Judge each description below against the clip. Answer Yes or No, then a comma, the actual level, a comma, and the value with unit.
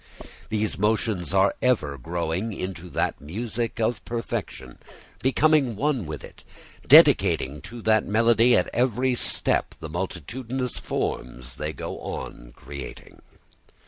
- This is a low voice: Yes, low, 105 Hz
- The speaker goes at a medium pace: No, slow, 120 wpm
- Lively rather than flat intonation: Yes, wide, 7.1 semitones